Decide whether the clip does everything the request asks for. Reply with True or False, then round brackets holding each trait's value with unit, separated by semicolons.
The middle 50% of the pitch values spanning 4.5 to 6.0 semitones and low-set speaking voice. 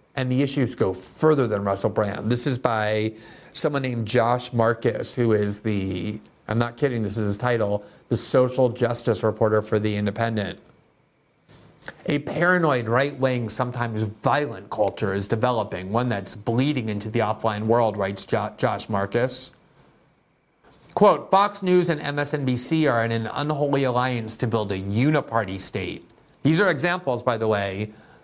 False (3.5 semitones; 115 Hz)